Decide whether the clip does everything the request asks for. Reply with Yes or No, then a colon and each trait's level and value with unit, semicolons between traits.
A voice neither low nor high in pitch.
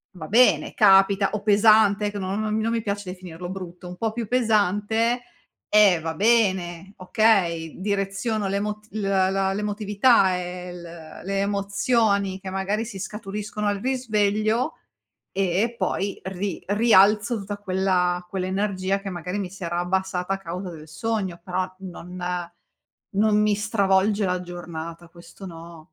No: high, 195 Hz